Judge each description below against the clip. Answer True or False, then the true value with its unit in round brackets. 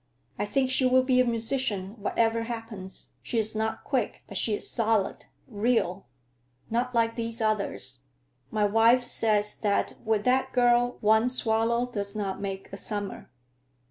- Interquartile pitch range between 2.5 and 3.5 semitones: True (2.8 semitones)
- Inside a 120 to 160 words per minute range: True (155 wpm)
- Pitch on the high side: True (225 Hz)